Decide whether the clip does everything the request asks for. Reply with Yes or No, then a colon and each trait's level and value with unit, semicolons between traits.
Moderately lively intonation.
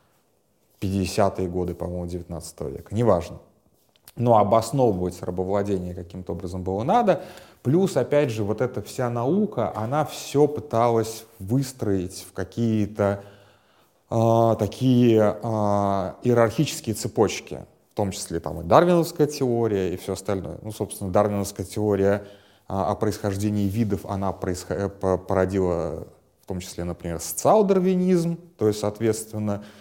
Yes: average, 3.9 semitones